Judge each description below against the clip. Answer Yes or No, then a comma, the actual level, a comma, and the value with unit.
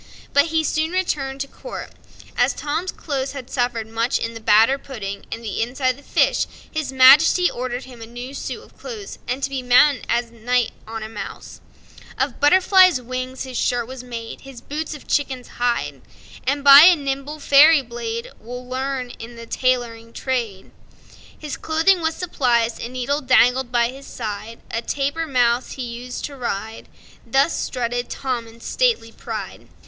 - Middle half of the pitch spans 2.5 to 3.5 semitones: Yes, average, 3.2 semitones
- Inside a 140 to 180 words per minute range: Yes, average, 175 wpm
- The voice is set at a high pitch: Yes, very high, 255 Hz